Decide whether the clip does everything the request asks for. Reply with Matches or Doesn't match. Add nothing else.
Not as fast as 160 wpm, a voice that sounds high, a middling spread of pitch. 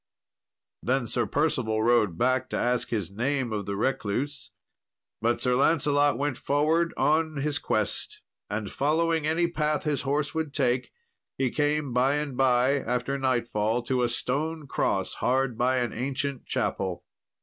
Doesn't match